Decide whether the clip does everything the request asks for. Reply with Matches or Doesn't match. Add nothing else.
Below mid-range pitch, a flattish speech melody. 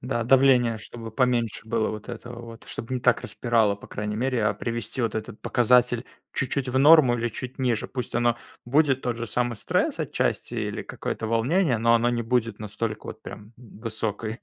Matches